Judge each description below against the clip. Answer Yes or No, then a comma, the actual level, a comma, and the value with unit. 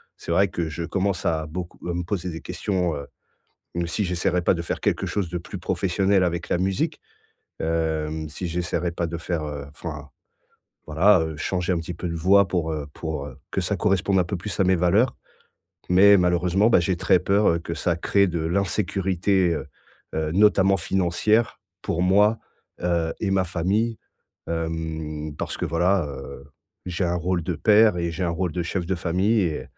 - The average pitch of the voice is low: Yes, very low, 90 Hz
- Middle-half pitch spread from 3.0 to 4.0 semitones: No, narrow, 2.5 semitones